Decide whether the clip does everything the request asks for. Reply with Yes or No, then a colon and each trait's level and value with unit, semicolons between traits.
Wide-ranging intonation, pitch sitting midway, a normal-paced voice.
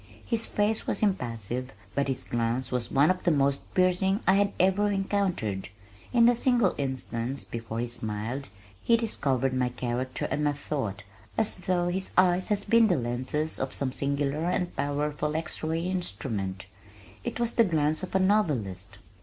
Yes: wide, 7.2 semitones; medium, 150 Hz; average, 170 wpm